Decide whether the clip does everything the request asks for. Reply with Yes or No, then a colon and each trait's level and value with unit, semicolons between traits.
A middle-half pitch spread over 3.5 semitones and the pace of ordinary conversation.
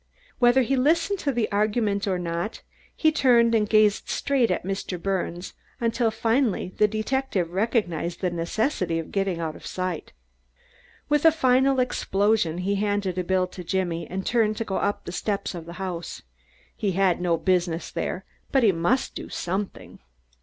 Yes: average, 4.5 semitones; average, 160 wpm